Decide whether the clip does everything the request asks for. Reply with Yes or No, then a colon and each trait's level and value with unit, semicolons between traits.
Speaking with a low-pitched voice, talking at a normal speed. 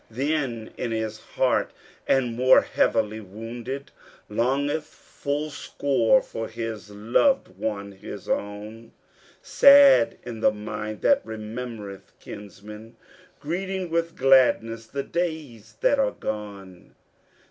No: low, 115 Hz; slow, 110 wpm